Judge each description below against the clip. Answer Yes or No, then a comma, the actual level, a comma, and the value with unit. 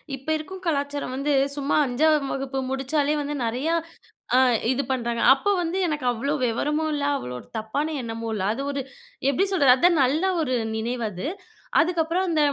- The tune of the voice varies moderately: Yes, average, 3.8 semitones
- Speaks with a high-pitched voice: Yes, very high, 280 Hz